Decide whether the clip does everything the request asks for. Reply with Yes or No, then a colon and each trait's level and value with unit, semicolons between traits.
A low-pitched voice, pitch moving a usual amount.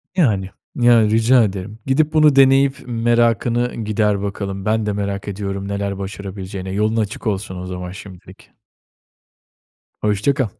Yes: low, 105 Hz; average, 3.2 semitones